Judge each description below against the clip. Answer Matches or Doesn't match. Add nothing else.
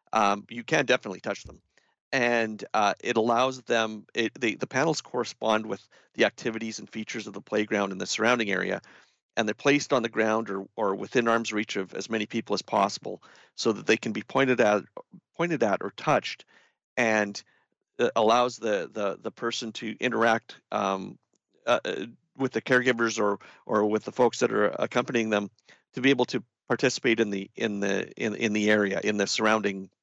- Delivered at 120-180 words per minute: Doesn't match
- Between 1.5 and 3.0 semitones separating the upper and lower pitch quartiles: Matches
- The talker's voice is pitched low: Matches